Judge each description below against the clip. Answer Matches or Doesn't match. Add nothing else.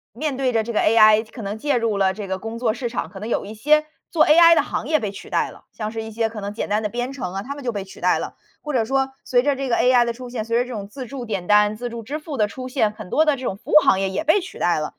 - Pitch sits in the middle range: Doesn't match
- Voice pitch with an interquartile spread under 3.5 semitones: Doesn't match